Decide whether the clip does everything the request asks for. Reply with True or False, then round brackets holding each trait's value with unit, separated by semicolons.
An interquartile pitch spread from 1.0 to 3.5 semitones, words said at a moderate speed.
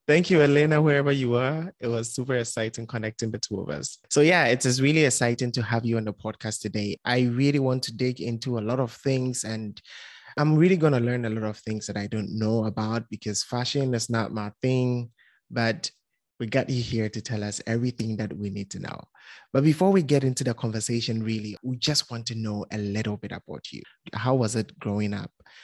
False (3.0 semitones; 225 wpm)